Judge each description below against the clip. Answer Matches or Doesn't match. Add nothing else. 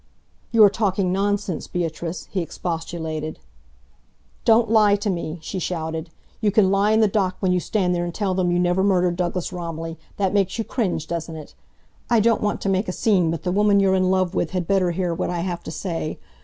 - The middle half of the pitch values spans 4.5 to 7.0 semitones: Doesn't match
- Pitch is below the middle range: Doesn't match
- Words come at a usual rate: Doesn't match